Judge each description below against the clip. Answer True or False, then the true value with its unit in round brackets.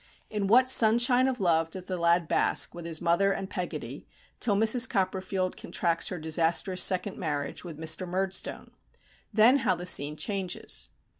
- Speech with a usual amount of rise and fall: True (3.8 semitones)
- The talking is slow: False (160 wpm)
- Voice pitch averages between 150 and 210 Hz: True (185 Hz)